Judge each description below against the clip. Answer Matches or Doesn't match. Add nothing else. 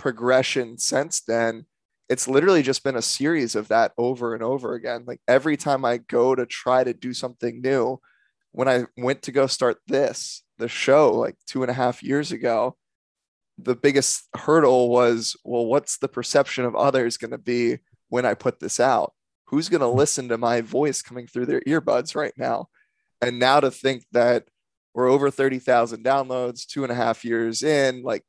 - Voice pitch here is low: Matches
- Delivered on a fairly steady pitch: Matches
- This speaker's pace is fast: Doesn't match